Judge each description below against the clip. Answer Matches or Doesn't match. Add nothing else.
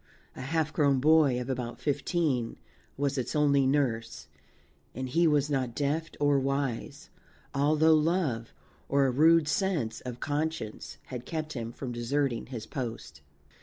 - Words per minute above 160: Doesn't match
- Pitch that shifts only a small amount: Doesn't match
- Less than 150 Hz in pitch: Matches